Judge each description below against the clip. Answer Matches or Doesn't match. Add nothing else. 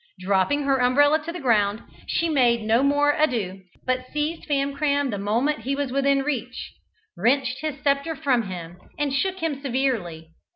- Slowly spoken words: Doesn't match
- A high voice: Matches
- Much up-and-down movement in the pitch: Doesn't match